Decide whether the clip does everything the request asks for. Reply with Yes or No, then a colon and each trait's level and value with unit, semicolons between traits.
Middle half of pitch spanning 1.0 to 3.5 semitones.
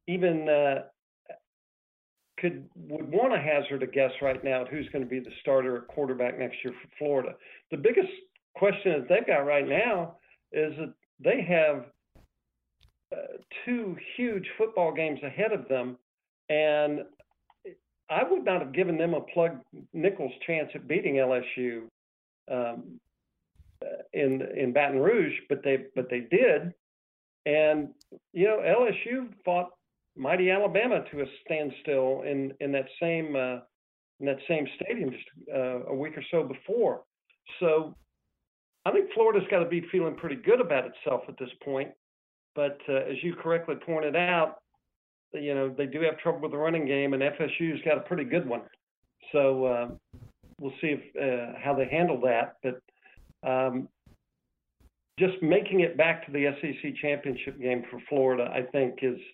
No: average, 4.5 semitones